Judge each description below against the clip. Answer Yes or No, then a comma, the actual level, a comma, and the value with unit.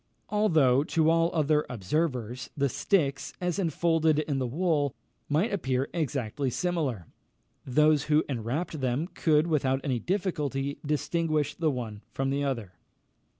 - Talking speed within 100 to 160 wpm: Yes, slow, 135 wpm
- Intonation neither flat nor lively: Yes, average, 3.6 semitones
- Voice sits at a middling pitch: Yes, medium, 150 Hz